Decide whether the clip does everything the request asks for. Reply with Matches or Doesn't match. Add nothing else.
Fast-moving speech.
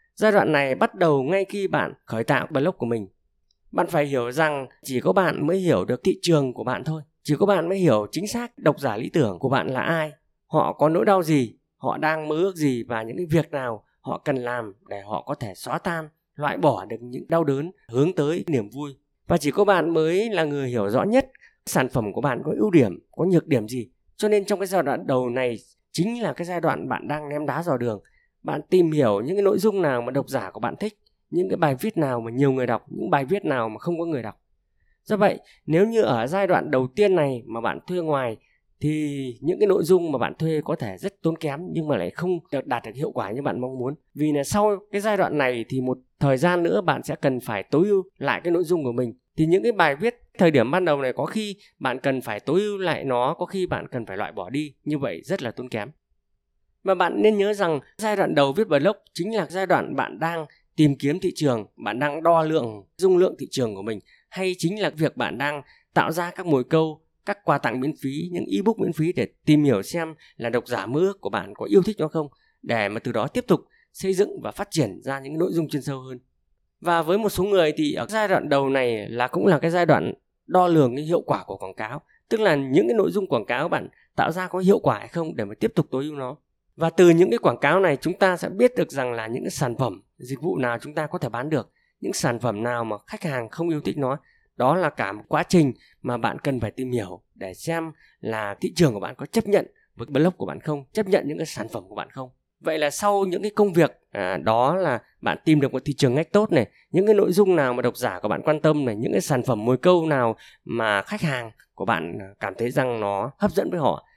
Matches